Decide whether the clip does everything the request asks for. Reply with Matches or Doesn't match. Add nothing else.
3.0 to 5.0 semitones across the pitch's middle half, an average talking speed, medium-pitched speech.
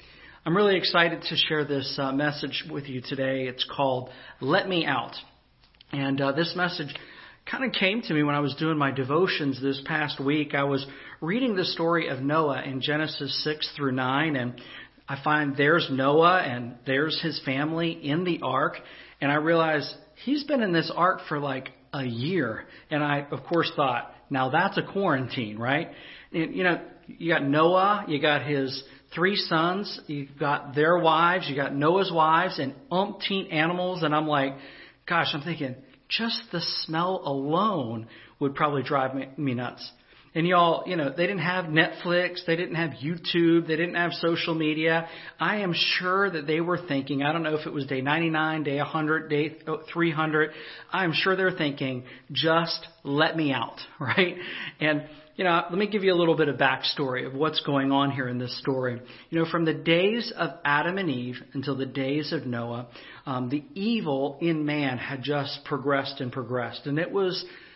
Matches